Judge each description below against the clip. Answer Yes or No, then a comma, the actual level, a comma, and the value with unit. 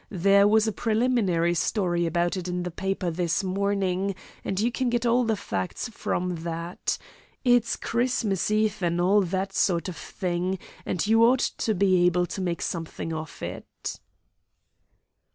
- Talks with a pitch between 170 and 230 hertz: Yes, high, 190 Hz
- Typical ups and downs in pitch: Yes, average, 3.6 semitones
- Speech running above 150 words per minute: Yes, average, 160 wpm